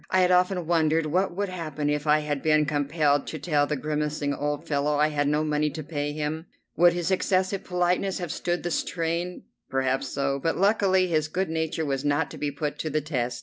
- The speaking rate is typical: No, fast, 215 wpm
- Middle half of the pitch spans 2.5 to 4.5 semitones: Yes, average, 3.1 semitones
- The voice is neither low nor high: Yes, medium, 155 Hz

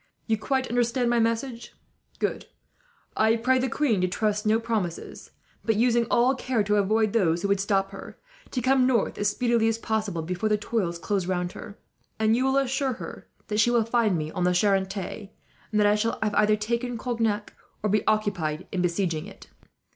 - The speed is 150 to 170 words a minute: No, average, 195 wpm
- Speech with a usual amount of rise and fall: Yes, average, 3.2 semitones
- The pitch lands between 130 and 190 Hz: No, high, 215 Hz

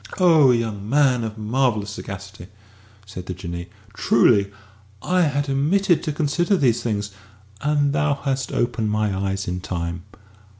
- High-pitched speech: No, low, 115 Hz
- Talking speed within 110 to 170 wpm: Yes, average, 140 wpm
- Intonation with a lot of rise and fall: Yes, wide, 6.3 semitones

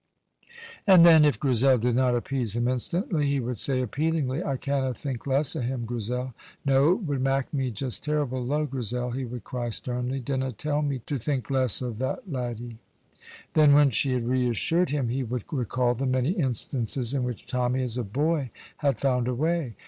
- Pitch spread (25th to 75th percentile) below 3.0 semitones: Yes, narrow, 2.5 semitones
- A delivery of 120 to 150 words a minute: No, average, 195 wpm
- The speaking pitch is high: No, low, 130 Hz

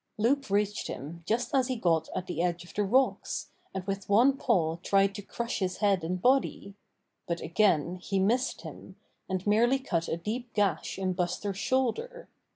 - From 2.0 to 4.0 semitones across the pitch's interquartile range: No, average, 5.0 semitones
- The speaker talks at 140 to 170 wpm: No, average, 180 wpm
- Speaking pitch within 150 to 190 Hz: No, high, 200 Hz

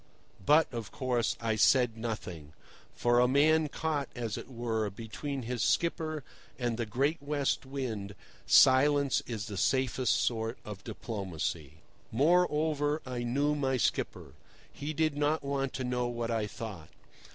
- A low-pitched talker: Yes, low, 125 Hz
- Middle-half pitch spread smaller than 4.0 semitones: No, average, 4.3 semitones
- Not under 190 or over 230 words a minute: No, average, 145 wpm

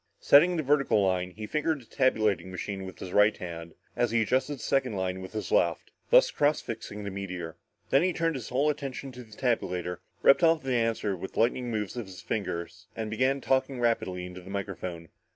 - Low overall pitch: Yes, low, 110 Hz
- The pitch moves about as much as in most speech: No, wide, 6.0 semitones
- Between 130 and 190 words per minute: No, fast, 205 wpm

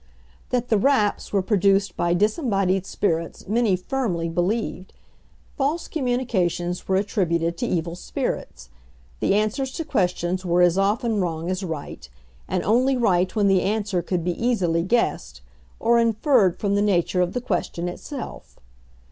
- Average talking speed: Yes, average, 150 wpm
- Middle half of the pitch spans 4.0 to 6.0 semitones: Yes, average, 4.6 semitones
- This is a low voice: No, high, 195 Hz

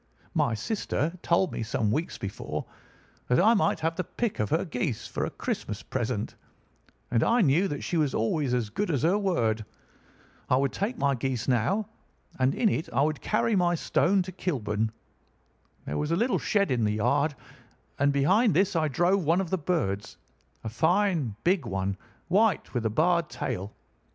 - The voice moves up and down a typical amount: No, wide, 7.4 semitones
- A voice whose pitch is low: No, medium, 155 Hz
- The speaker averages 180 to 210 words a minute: Yes, average, 185 wpm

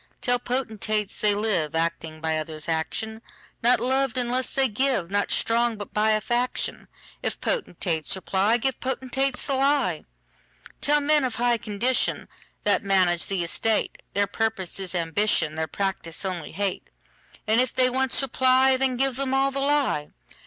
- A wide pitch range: Yes, wide, 5.8 semitones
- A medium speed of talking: No, slow, 125 wpm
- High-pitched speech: Yes, high, 220 Hz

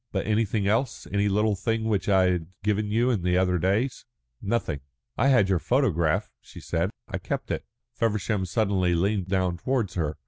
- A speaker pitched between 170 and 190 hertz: No, low, 100 Hz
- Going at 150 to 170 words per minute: No, average, 180 wpm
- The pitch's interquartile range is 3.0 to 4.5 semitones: Yes, average, 3.4 semitones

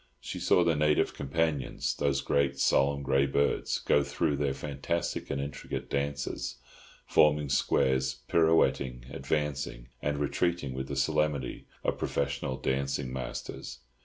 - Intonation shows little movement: Yes, narrow, 1.7 semitones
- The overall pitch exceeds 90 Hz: No, very low, 70 Hz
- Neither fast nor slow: No, slow, 130 wpm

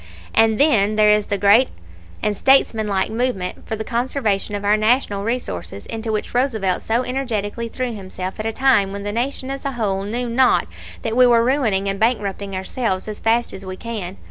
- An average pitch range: Yes, average, 3.4 semitones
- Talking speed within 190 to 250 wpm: Yes, average, 195 wpm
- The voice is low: No, high, 220 Hz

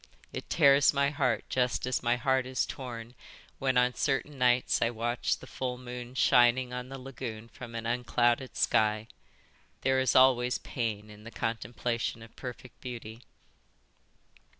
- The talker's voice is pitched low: Yes, low, 125 Hz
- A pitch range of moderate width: No, narrow, 1.9 semitones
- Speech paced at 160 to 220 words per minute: No, average, 150 wpm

